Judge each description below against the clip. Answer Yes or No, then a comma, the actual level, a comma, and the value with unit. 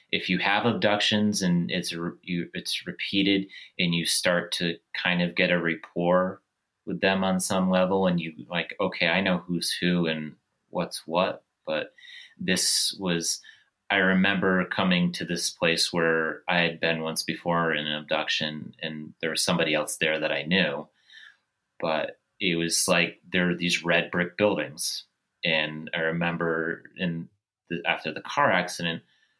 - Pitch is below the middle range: Yes, very low, 85 Hz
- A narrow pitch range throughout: Yes, narrow, 2.2 semitones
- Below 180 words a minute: Yes, average, 165 wpm